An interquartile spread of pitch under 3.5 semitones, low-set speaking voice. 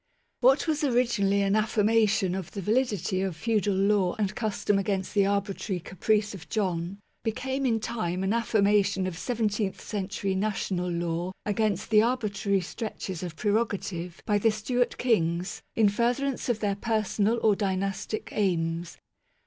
No: average, 2.8 semitones; high, 205 Hz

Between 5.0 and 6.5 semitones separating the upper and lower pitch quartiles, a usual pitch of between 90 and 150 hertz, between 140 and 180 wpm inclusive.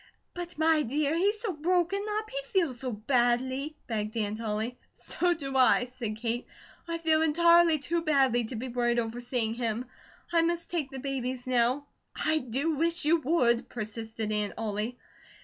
No: wide, 5.6 semitones; very high, 260 Hz; average, 170 wpm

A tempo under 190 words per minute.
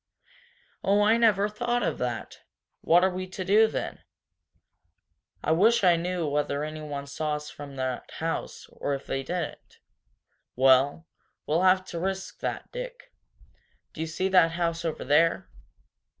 Yes: average, 150 wpm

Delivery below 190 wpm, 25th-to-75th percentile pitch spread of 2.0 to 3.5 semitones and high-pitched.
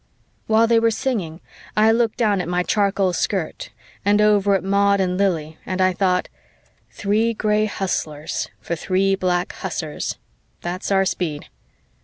Yes: average, 155 wpm; average, 2.8 semitones; high, 195 Hz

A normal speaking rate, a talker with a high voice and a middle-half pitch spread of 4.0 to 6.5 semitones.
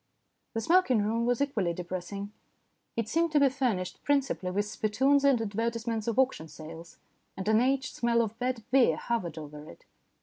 Yes: average, 170 wpm; high, 225 Hz; average, 5.1 semitones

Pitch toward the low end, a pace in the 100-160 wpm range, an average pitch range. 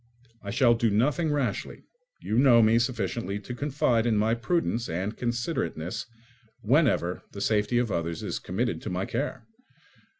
Yes: low, 115 Hz; average, 155 wpm; average, 3.8 semitones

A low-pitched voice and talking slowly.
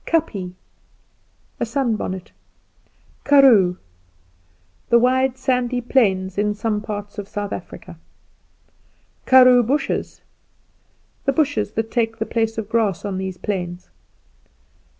No: high, 225 Hz; slow, 110 wpm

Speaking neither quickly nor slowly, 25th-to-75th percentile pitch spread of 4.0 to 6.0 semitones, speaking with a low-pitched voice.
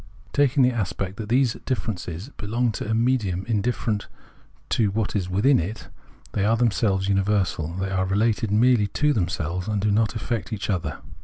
No: average, 170 wpm; average, 3.5 semitones; low, 105 Hz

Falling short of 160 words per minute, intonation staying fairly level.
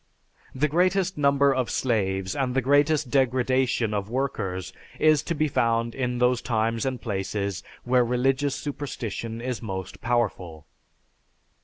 No: slow, 135 wpm; average, 3.8 semitones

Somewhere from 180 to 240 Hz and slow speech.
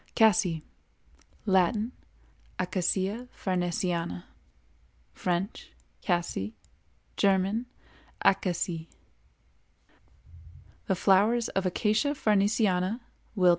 Yes: high, 190 Hz; slow, 50 wpm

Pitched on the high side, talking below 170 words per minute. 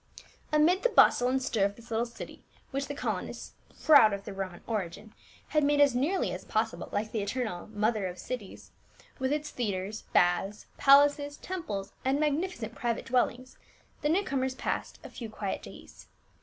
No: high, 245 Hz; average, 175 wpm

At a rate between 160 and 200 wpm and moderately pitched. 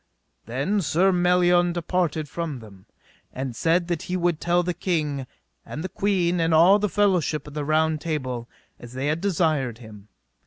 Yes: average, 170 wpm; medium, 165 Hz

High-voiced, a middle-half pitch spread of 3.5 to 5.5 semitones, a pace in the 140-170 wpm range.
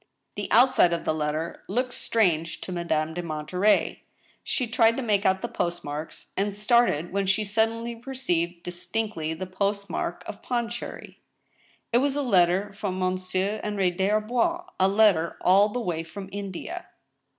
Yes: high, 195 Hz; average, 4.4 semitones; average, 165 wpm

